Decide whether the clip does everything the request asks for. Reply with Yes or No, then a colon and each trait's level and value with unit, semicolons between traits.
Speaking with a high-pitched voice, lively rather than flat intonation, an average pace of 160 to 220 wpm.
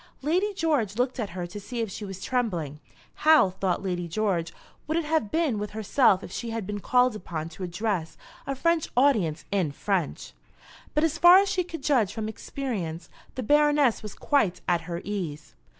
Yes: high, 215 Hz; wide, 7.8 semitones; average, 190 wpm